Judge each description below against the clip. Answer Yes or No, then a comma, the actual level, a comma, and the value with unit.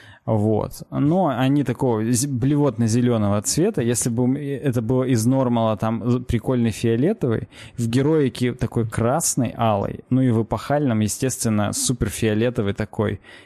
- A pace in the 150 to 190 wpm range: No, average, 125 wpm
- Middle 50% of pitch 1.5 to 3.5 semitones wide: Yes, average, 2.8 semitones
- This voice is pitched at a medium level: No, low, 120 Hz